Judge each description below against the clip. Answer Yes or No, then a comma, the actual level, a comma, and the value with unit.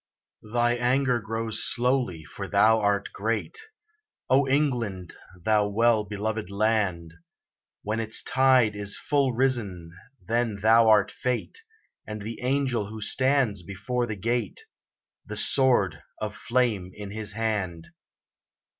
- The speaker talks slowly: Yes, slow, 125 wpm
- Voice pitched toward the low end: Yes, low, 110 Hz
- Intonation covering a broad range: No, average, 3.2 semitones